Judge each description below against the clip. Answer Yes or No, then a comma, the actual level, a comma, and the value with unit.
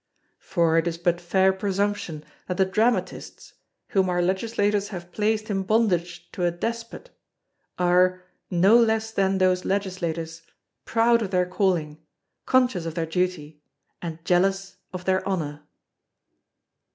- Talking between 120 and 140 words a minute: Yes, slow, 135 wpm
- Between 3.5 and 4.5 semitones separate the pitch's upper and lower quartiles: No, average, 2.9 semitones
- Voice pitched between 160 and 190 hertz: Yes, medium, 185 Hz